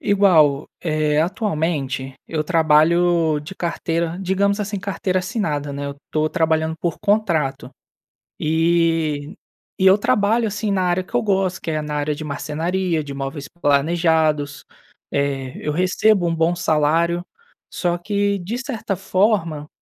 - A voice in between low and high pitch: Yes, medium, 165 Hz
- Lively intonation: No, average, 3.9 semitones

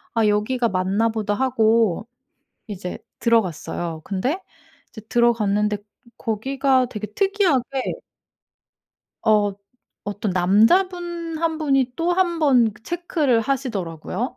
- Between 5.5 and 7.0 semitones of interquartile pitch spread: No, average, 5.1 semitones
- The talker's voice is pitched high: Yes, high, 230 Hz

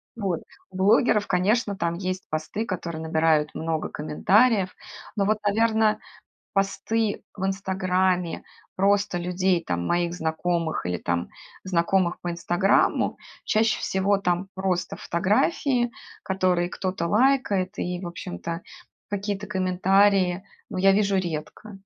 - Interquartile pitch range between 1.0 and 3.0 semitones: Yes, average, 2.7 semitones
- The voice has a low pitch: No, medium, 185 Hz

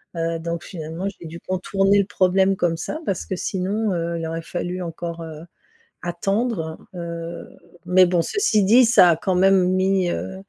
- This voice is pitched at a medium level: Yes, medium, 180 Hz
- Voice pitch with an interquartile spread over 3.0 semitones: No, narrow, 2.5 semitones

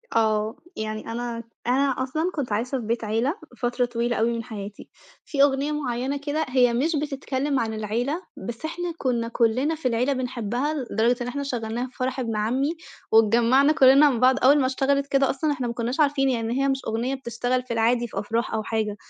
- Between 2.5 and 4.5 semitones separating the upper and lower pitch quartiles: Yes, average, 3.2 semitones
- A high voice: Yes, very high, 250 Hz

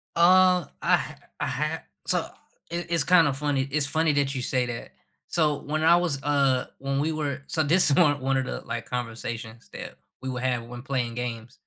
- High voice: No, medium, 140 Hz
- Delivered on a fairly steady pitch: No, average, 4.0 semitones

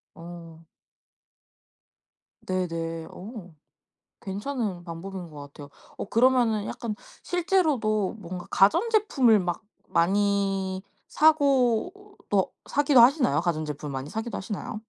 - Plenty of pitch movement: Yes, wide, 6.1 semitones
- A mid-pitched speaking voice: No, high, 200 Hz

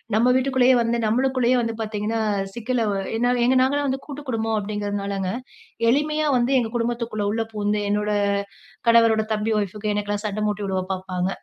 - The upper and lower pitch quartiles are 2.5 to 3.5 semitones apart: Yes, average, 3.0 semitones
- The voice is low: No, high, 225 Hz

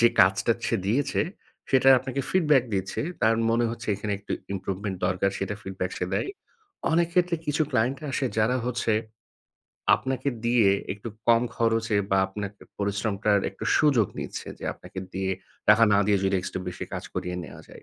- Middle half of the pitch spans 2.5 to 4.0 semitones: No, average, 4.7 semitones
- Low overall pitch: Yes, low, 110 Hz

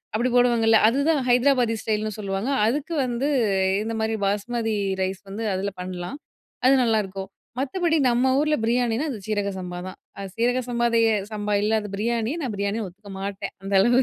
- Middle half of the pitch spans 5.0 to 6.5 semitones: No, average, 3.5 semitones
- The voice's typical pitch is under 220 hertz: No, high, 225 Hz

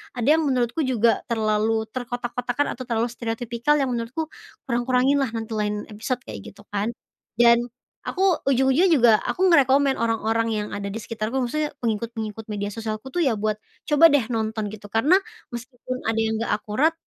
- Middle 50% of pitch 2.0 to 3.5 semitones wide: Yes, average, 3.0 semitones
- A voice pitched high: Yes, high, 235 Hz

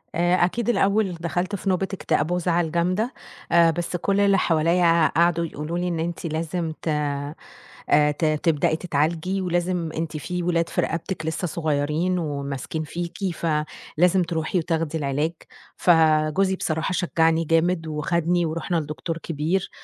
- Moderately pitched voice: Yes, medium, 165 Hz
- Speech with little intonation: Yes, narrow, 2.2 semitones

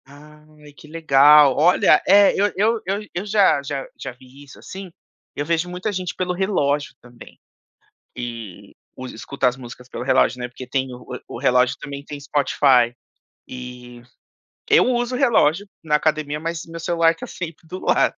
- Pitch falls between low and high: Yes, medium, 150 Hz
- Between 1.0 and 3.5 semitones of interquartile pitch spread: No, wide, 5.4 semitones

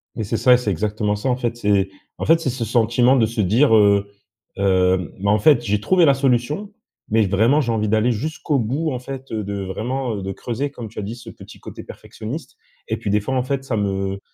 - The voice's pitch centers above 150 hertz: No, low, 115 Hz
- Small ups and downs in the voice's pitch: No, average, 4.2 semitones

